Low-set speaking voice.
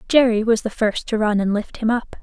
No: high, 220 Hz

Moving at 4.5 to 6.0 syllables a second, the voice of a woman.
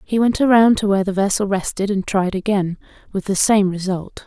Yes: 5.5 syllables/s; female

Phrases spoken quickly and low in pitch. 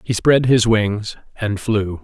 No: average, 175 wpm; low, 110 Hz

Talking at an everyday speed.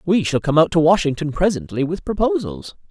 Yes: average, 185 wpm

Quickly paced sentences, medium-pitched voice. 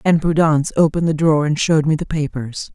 Yes: fast, 220 wpm; medium, 155 Hz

